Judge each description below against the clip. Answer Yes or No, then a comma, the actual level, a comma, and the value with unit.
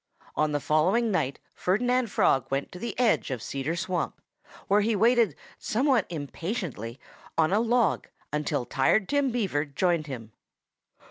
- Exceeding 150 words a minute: No, average, 145 wpm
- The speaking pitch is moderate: Yes, medium, 180 Hz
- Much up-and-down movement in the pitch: Yes, wide, 7.8 semitones